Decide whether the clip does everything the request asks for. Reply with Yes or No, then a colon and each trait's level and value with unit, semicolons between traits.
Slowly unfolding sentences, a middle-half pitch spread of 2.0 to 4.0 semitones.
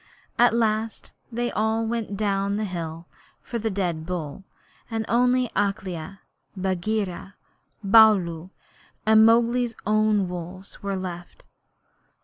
Yes: slow, 115 wpm; average, 3.4 semitones